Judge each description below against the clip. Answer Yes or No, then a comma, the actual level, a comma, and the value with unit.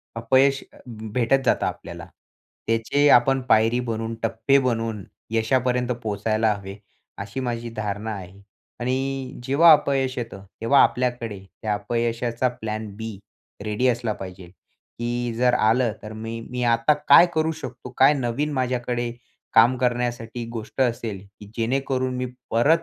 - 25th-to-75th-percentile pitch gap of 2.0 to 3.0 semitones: Yes, narrow, 2.5 semitones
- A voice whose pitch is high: No, low, 120 Hz